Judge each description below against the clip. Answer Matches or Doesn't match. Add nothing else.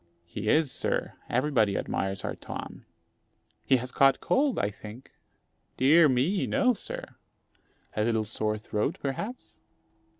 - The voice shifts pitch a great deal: Matches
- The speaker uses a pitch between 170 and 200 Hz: Doesn't match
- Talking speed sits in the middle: Doesn't match